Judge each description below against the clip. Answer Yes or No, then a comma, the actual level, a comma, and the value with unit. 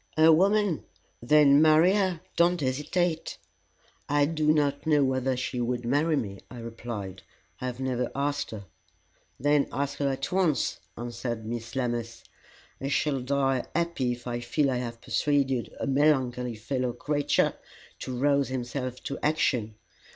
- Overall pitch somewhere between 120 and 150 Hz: Yes, low, 135 Hz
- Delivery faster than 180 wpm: No, average, 150 wpm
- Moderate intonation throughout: Yes, average, 3.4 semitones